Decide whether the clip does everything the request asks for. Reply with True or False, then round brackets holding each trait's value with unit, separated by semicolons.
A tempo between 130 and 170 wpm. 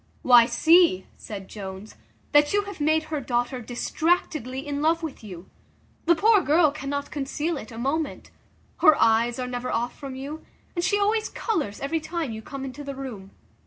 False (180 wpm)